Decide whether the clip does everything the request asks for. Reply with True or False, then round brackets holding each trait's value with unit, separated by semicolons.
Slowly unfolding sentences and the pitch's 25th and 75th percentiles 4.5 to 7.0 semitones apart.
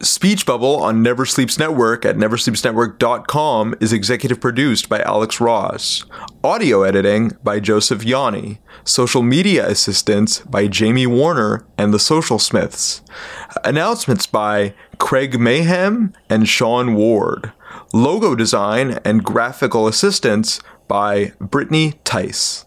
False (115 wpm; 4.1 semitones)